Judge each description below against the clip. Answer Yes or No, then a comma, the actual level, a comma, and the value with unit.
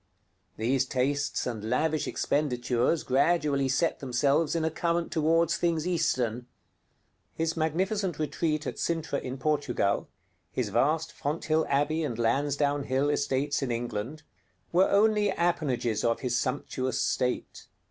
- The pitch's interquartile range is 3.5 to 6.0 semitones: Yes, average, 4.1 semitones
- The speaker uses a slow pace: Yes, slow, 125 wpm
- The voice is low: No, medium, 145 Hz